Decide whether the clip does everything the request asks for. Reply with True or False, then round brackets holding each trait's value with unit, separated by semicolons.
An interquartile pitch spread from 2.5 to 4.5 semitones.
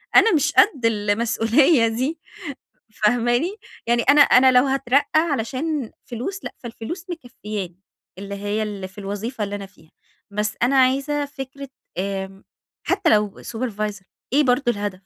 False (5.1 semitones)